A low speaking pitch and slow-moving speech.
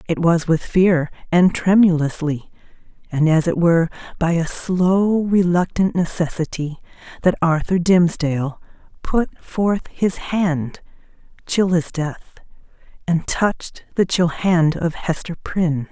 No: medium, 170 Hz; slow, 125 wpm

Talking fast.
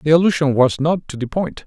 Yes: fast, 250 wpm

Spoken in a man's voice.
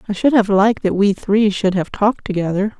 No: female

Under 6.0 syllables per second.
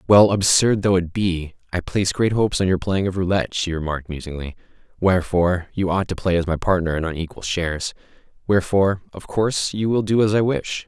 No: 6.1 syllables/s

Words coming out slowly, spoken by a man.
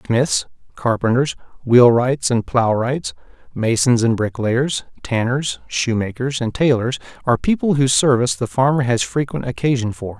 Yes: slow, 130 wpm; male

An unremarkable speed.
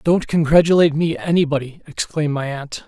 Yes: average, 145 wpm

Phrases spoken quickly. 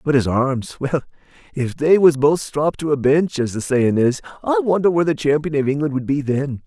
Yes: fast, 225 wpm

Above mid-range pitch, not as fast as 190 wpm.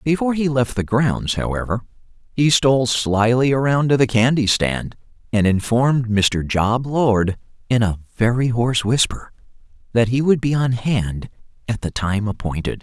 No: low, 120 Hz; average, 160 wpm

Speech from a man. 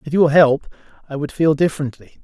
Yes: male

